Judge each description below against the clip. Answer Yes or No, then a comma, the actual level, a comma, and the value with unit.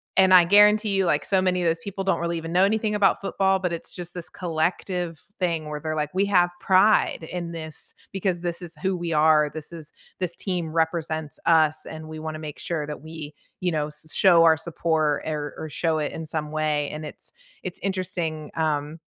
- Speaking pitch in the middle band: Yes, medium, 165 Hz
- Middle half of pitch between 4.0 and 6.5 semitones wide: No, average, 2.7 semitones